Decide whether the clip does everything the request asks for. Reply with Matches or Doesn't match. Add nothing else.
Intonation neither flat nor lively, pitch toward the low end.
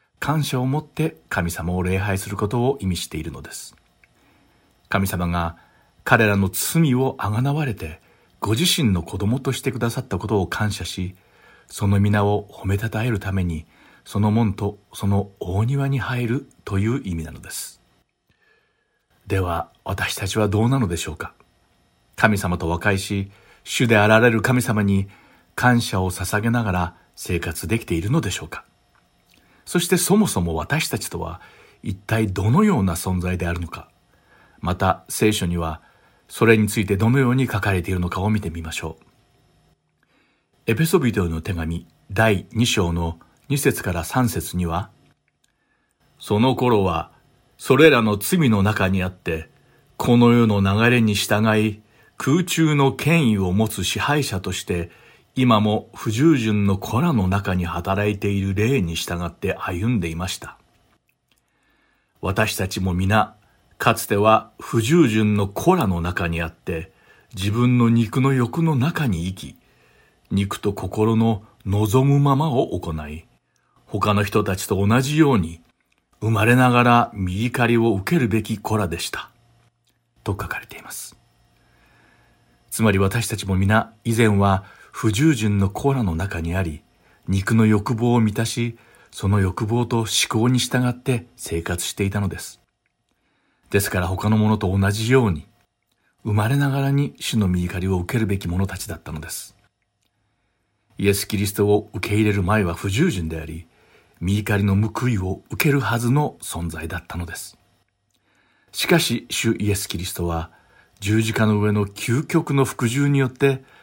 Matches